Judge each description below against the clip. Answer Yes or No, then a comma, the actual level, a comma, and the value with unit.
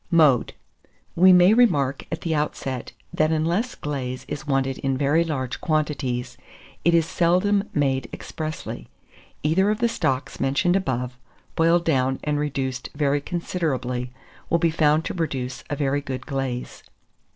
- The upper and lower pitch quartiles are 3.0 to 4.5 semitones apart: Yes, average, 4.0 semitones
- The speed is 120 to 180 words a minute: Yes, average, 145 wpm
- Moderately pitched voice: Yes, medium, 150 Hz